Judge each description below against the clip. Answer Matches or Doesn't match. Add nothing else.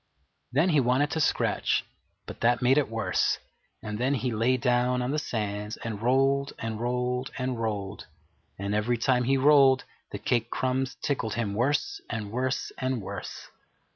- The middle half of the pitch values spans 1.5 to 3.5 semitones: Matches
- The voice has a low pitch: Matches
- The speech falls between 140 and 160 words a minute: Doesn't match